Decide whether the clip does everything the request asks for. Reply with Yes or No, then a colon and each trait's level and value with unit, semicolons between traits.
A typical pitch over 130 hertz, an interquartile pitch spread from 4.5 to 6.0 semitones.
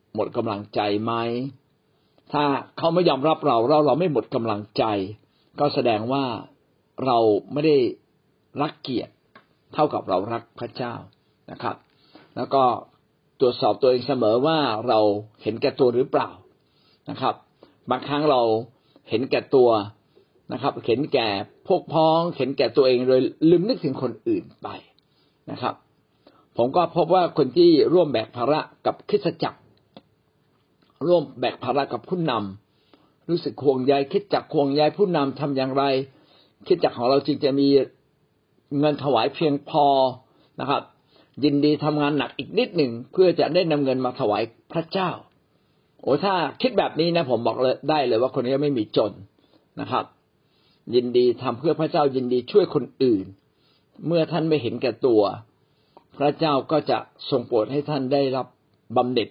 No: medium, 140 Hz; average, 3.6 semitones